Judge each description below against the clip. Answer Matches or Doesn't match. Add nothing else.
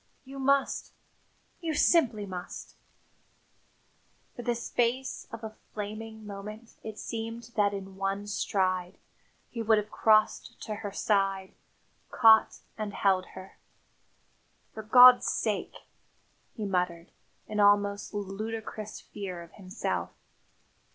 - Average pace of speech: Doesn't match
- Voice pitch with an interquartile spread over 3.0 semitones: Doesn't match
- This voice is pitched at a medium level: Doesn't match